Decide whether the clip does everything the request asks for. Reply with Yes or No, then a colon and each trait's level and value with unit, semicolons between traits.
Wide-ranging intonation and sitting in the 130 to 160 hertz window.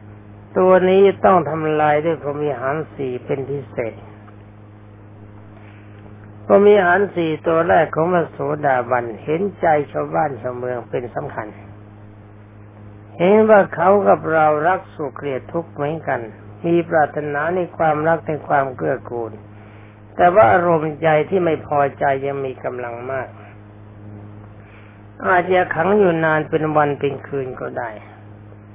Yes: wide, 7.4 semitones; low, 135 Hz